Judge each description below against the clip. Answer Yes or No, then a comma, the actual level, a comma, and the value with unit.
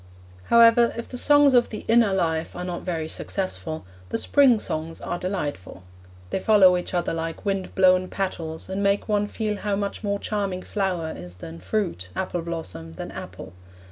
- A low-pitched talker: No, medium, 185 Hz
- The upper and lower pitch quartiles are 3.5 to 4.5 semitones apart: Yes, average, 4.1 semitones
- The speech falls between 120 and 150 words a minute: No, average, 175 wpm